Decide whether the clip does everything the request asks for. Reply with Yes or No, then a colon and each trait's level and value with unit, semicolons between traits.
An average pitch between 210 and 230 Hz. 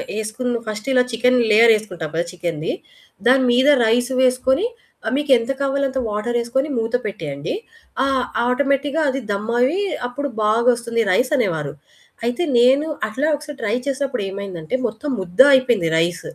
No: high, 240 Hz